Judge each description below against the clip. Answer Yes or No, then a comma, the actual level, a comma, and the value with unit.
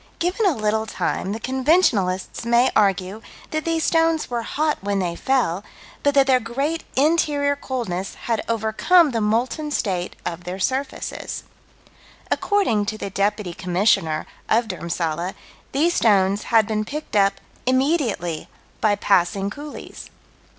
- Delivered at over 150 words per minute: No, slow, 135 wpm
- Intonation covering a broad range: Yes, wide, 6.5 semitones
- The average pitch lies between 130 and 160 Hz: No, high, 225 Hz